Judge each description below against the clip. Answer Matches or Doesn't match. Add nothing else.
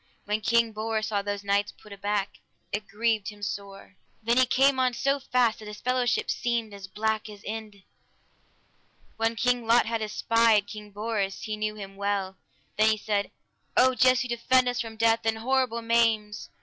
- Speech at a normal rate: Matches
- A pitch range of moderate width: Doesn't match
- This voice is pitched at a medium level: Doesn't match